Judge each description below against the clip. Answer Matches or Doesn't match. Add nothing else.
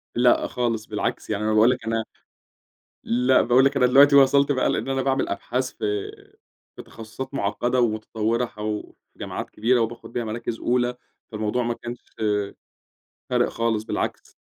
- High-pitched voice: Doesn't match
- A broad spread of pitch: Doesn't match